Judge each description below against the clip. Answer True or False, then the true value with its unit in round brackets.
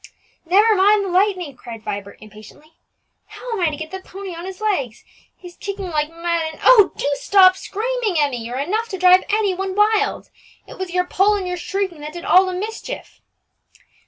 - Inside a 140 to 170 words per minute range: False (195 wpm)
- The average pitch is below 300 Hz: False (370 Hz)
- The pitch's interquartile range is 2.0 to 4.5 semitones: True (4.2 semitones)